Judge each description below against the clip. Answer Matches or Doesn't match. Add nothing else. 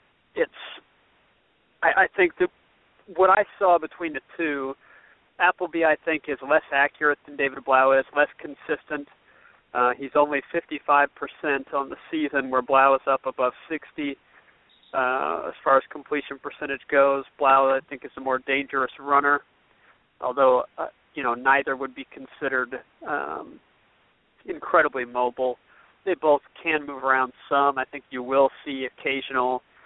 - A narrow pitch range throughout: Matches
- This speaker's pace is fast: Doesn't match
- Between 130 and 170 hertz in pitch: Matches